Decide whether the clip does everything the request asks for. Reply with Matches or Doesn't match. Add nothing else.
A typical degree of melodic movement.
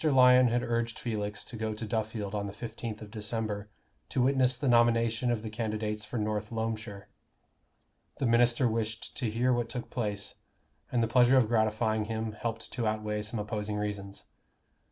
Doesn't match